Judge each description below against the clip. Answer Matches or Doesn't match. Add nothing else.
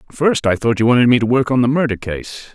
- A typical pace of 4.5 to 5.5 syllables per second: Doesn't match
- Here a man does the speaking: Matches